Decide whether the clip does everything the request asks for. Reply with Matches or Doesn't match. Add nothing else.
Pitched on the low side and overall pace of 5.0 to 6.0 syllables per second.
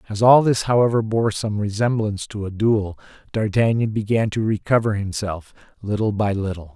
Matches